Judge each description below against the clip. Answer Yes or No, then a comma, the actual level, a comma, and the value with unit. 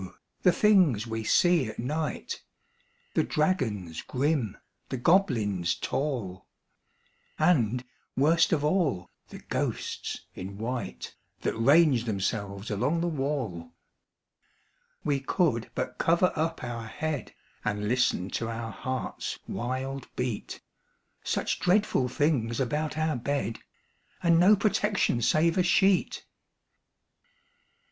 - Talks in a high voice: No, low, 130 Hz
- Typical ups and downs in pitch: No, wide, 6.2 semitones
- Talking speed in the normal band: No, slow, 110 wpm